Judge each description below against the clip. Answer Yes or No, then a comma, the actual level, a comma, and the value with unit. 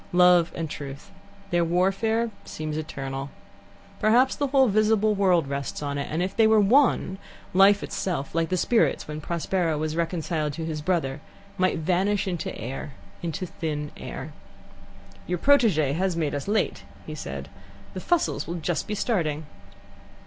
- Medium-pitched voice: Yes, medium, 175 Hz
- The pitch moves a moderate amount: Yes, average, 4.7 semitones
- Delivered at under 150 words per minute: No, average, 155 wpm